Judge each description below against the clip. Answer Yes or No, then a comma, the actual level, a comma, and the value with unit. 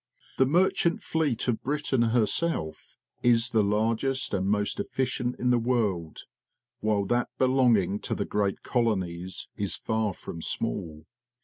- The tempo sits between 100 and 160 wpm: Yes, slow, 135 wpm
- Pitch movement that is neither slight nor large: Yes, average, 4.3 semitones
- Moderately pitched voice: No, low, 115 Hz